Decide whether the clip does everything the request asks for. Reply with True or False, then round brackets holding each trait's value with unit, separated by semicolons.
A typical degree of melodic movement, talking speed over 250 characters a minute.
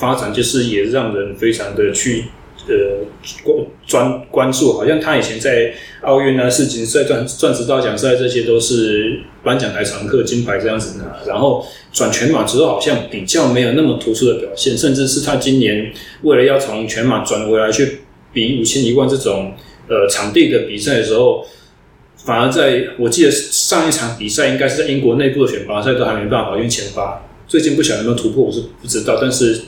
False (5.9 semitones; 300 characters per minute)